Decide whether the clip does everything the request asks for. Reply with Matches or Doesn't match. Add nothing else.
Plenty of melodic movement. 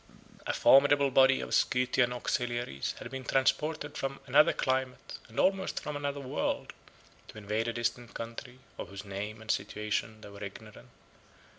Doesn't match